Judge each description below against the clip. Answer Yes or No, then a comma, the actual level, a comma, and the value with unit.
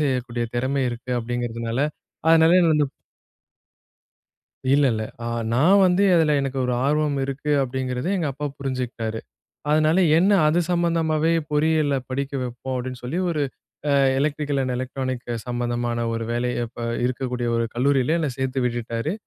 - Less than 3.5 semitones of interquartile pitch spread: No, average, 3.8 semitones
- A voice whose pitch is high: No, low, 130 Hz